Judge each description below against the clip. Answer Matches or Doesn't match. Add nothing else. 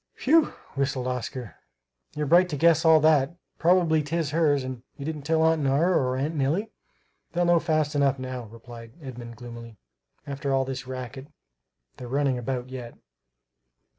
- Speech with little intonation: Doesn't match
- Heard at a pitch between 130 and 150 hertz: Matches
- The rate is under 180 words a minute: Matches